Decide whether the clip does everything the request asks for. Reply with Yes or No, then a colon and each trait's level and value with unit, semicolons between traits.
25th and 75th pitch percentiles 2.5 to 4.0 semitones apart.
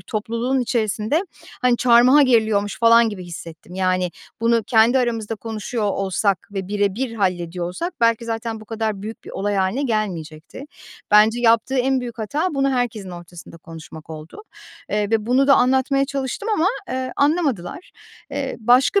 No: average, 4.4 semitones